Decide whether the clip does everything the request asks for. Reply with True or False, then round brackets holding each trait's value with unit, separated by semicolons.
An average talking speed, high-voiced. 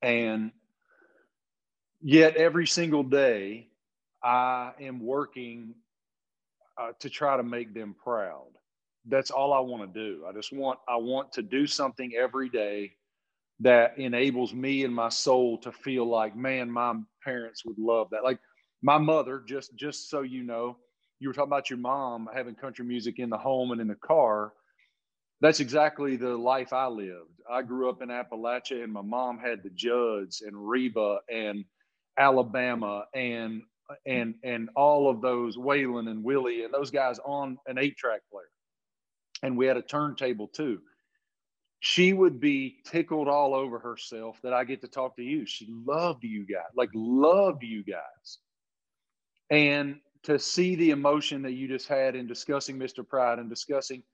False (165 wpm; 125 Hz)